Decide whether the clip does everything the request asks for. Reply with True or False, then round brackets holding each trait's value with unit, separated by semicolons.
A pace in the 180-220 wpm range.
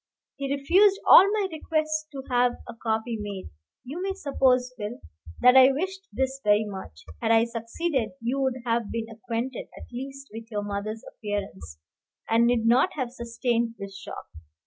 False (170 wpm)